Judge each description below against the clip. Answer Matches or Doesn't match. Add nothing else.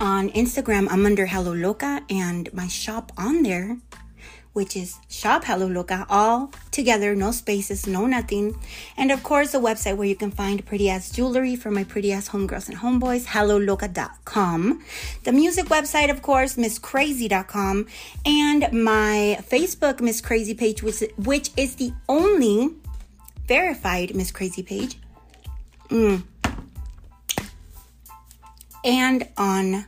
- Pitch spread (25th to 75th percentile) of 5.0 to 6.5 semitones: Doesn't match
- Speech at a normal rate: Doesn't match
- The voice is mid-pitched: Doesn't match